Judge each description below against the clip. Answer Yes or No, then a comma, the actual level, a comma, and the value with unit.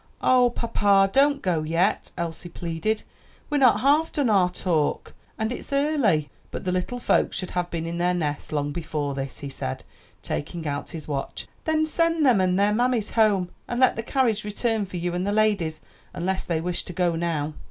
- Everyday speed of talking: Yes, average, 195 wpm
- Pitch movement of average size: No, wide, 5.9 semitones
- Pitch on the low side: No, medium, 185 Hz